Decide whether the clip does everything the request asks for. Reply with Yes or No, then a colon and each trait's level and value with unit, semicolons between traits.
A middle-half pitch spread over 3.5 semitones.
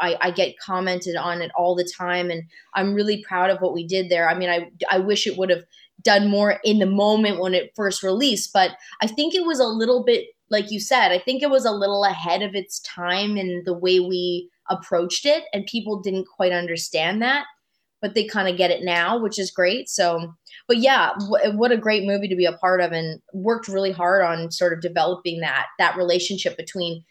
No: average, 2.9 semitones